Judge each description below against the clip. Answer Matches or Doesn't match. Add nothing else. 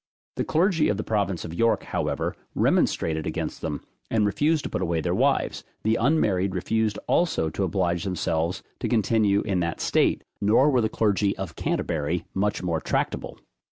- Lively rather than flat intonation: Doesn't match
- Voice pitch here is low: Matches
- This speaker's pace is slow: Doesn't match